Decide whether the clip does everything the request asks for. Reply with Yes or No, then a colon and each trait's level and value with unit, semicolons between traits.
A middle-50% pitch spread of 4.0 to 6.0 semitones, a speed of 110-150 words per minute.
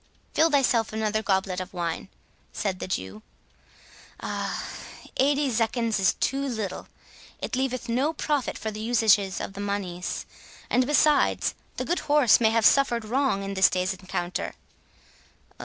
Yes: average, 5.2 semitones; average, 145 wpm